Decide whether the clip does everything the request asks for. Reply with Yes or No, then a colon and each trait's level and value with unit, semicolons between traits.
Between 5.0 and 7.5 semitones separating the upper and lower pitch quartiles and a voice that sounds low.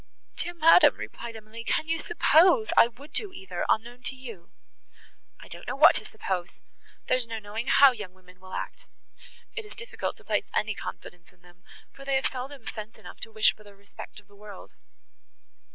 No: wide, 5.4 semitones; high, 225 Hz